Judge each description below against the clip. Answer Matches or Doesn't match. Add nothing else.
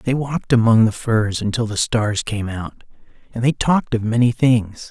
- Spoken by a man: Matches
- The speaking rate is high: Doesn't match